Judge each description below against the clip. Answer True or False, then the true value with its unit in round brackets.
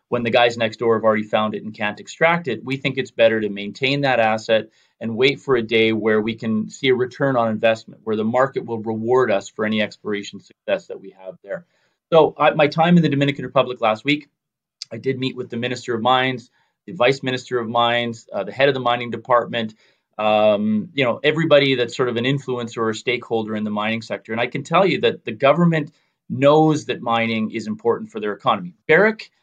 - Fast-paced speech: True (225 wpm)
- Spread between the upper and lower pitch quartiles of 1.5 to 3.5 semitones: False (3.9 semitones)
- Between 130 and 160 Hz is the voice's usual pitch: False (120 Hz)